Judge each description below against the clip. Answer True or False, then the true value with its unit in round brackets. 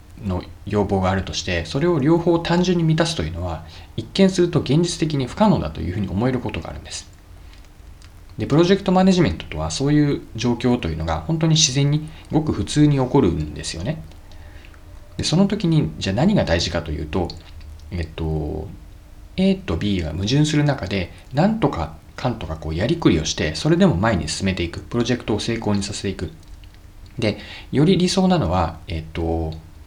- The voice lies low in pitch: True (95 Hz)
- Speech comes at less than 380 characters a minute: False (400 characters per minute)